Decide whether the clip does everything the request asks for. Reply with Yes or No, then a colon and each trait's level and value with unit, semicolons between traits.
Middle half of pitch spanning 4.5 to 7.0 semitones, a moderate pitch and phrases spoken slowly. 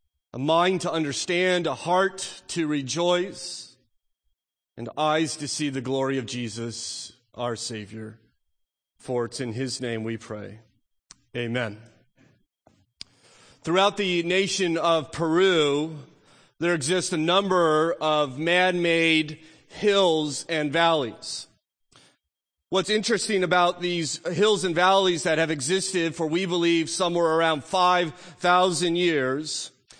Yes: wide, 5.5 semitones; medium, 160 Hz; slow, 120 wpm